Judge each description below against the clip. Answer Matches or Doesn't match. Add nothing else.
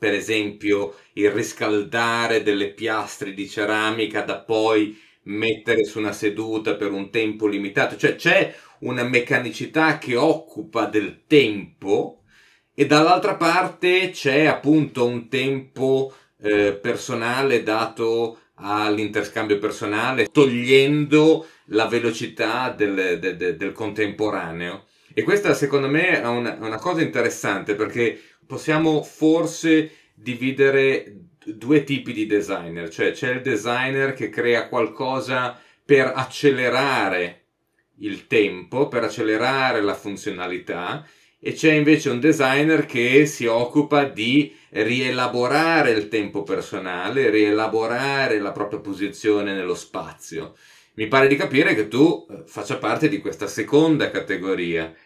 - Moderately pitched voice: Doesn't match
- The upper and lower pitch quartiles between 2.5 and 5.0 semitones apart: Doesn't match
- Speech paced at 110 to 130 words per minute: Matches